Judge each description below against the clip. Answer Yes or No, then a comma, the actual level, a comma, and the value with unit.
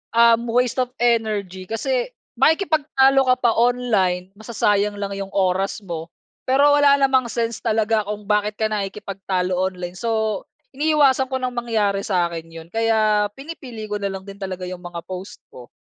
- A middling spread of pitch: Yes, average, 4.3 semitones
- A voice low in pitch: No, high, 215 Hz